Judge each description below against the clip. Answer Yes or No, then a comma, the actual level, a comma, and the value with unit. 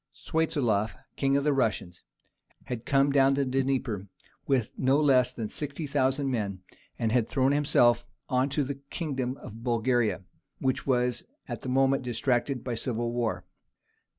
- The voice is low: Yes, low, 130 Hz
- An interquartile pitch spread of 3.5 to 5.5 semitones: No, narrow, 2.6 semitones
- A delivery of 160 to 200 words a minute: No, average, 150 wpm